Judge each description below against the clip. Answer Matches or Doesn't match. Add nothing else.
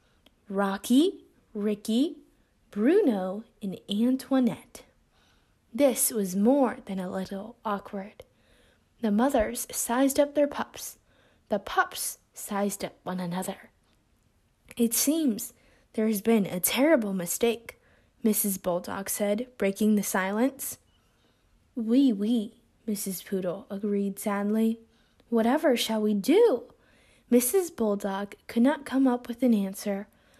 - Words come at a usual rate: Doesn't match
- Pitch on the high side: Matches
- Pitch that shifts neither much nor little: Matches